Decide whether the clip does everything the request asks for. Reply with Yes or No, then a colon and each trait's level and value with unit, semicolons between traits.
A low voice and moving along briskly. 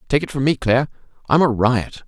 Yes: low, 130 Hz; fast, 230 wpm